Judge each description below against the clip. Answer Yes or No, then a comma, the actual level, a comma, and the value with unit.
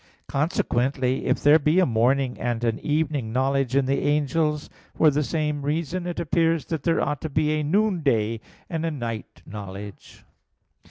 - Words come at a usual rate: Yes, average, 165 wpm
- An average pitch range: Yes, average, 4.0 semitones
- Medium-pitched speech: Yes, medium, 145 Hz